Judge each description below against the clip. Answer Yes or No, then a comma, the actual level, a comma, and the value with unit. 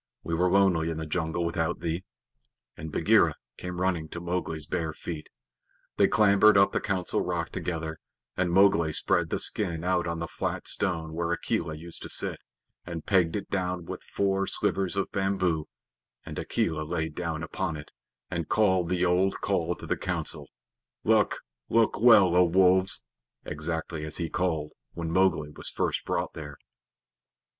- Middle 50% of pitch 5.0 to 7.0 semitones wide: No, narrow, 2.6 semitones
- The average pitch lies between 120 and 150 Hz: No, very low, 85 Hz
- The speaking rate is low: No, average, 165 wpm